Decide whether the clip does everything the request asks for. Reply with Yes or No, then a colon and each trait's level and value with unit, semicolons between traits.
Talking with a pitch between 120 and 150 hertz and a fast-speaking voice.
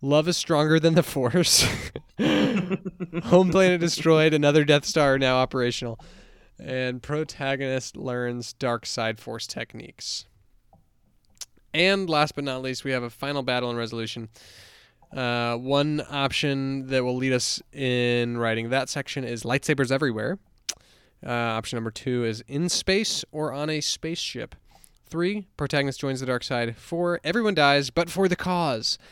No: low, 135 Hz; average, 150 wpm